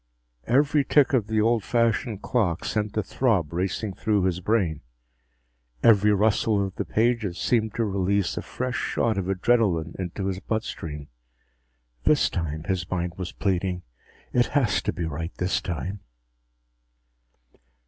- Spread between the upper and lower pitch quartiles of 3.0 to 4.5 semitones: Yes, average, 4.0 semitones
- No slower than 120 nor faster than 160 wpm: Yes, average, 150 wpm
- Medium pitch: No, low, 100 Hz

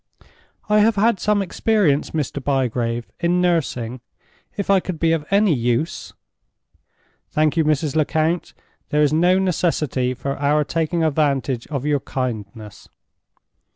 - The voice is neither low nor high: Yes, medium, 150 Hz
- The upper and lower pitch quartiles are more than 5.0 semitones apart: No, average, 4.7 semitones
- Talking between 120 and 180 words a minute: Yes, slow, 135 wpm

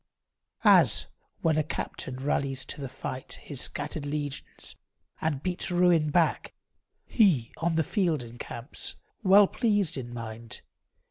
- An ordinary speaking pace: No, slow, 130 wpm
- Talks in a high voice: No, medium, 150 Hz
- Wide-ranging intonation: No, average, 5.0 semitones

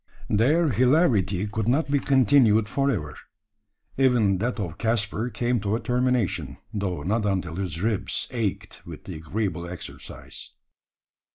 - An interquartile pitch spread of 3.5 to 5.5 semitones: Yes, average, 4.6 semitones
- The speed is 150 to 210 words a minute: No, average, 140 wpm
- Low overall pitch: Yes, low, 110 Hz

